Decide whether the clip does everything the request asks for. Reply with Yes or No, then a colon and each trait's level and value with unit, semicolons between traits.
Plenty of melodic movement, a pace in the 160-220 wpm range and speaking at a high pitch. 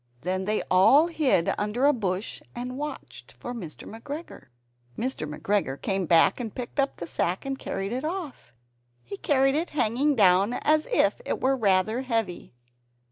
Yes: wide, 6.3 semitones; average, 165 wpm; high, 230 Hz